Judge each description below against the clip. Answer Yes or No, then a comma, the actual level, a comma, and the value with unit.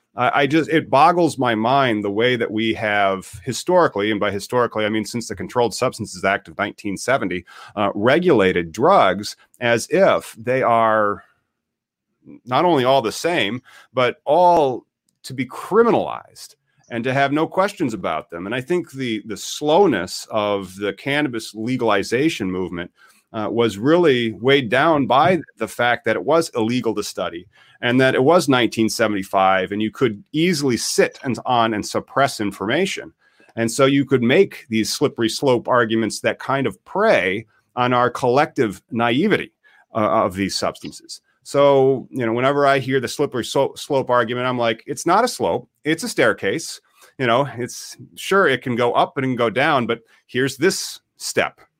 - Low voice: Yes, low, 120 Hz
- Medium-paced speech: Yes, average, 170 wpm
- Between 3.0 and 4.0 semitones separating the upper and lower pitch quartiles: Yes, average, 3.7 semitones